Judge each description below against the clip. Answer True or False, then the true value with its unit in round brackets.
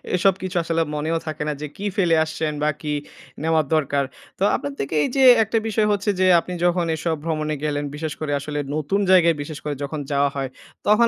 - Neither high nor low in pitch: True (160 Hz)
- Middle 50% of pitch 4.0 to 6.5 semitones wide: False (3.4 semitones)